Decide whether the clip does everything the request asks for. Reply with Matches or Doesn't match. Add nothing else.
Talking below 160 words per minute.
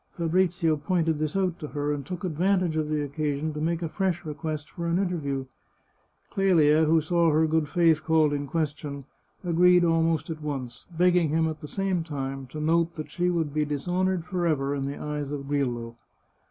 Doesn't match